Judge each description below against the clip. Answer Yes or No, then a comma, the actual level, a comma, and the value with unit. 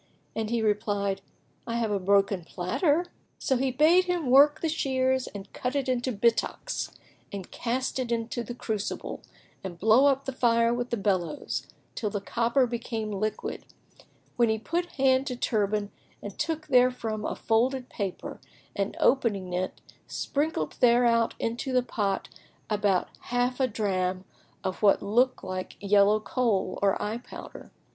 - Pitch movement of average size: Yes, average, 4.2 semitones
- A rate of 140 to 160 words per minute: Yes, average, 150 wpm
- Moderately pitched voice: No, high, 230 Hz